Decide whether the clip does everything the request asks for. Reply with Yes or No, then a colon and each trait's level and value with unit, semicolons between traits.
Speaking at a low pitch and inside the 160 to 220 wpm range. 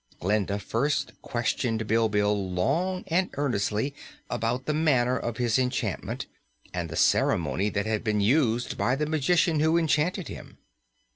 No: low, 120 Hz; average, 140 wpm